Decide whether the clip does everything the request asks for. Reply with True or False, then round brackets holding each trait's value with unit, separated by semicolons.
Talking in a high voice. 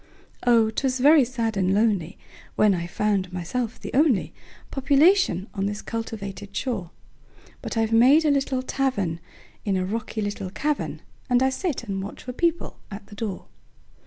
True (225 Hz)